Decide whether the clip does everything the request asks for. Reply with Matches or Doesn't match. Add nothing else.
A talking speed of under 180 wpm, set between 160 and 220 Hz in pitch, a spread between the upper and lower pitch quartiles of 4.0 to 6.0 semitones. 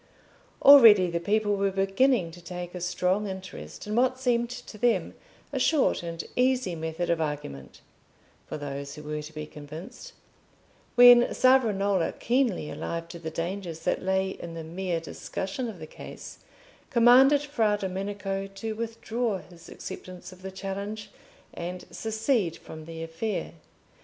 Matches